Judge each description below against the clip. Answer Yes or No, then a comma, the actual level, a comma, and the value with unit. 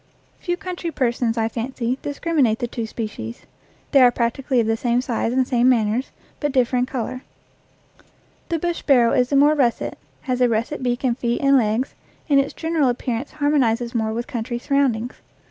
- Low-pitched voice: No, very high, 250 Hz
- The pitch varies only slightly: No, average, 3.0 semitones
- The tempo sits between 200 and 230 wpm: No, average, 180 wpm